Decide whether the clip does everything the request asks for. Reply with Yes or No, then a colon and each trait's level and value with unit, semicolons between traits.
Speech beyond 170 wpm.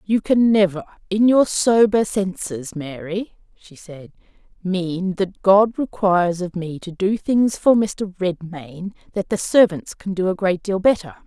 No: average, 165 wpm